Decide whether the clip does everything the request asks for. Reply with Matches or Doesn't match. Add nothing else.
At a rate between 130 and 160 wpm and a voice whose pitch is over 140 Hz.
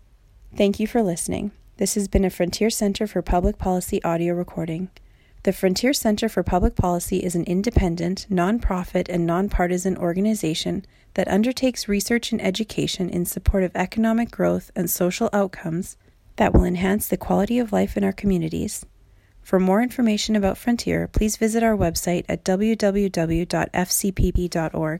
Matches